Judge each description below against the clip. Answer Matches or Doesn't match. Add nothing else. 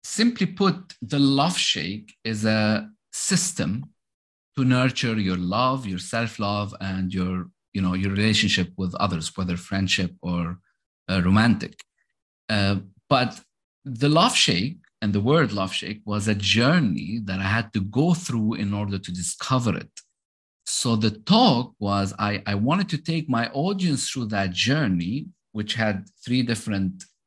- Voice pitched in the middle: Doesn't match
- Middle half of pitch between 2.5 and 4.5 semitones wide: Doesn't match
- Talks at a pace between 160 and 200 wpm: Doesn't match